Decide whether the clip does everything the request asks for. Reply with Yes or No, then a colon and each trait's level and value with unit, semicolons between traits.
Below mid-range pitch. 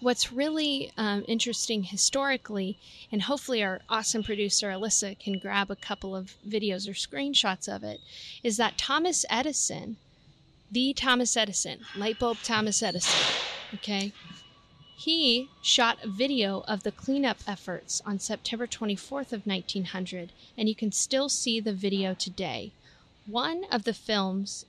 No: high, 210 Hz